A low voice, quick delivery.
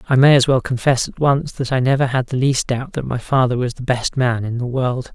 Yes: low, 130 Hz; fast, 280 wpm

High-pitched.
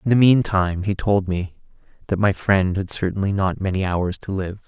No: very low, 95 Hz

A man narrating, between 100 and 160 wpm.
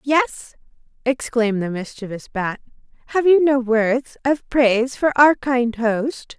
No: female; average, 140 wpm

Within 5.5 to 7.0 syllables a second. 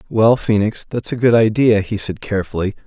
Yes: 5.6 syllables/s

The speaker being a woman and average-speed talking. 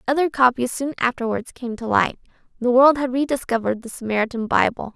Yes: female; average, 170 wpm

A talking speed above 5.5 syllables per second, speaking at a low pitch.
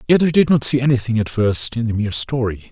Yes: 6.3 syllables/s; low, 120 Hz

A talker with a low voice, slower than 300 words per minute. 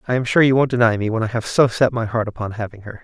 No: low, 115 Hz; fast, 335 wpm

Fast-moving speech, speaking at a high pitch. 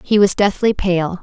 No: average, 195 wpm; high, 195 Hz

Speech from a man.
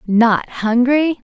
No: female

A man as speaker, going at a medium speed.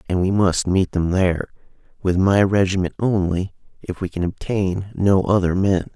Yes: male; average, 170 wpm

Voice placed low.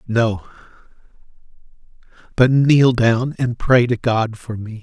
Yes: low, 120 Hz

